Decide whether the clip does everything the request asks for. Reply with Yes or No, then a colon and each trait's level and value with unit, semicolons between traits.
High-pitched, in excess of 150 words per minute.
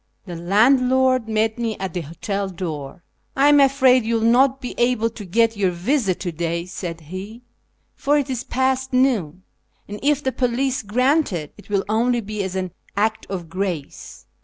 Yes: high, 220 Hz; average, 190 wpm